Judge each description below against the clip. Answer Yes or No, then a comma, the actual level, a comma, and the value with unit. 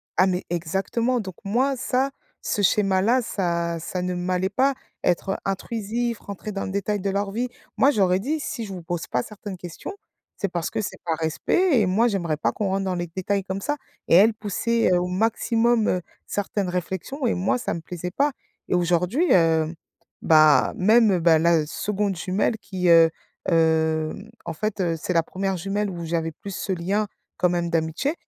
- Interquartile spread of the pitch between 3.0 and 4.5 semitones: Yes, average, 3.7 semitones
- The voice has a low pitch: No, high, 190 Hz